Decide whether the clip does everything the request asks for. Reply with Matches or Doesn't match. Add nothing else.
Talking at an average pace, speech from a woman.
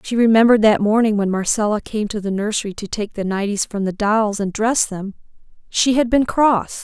Doesn't match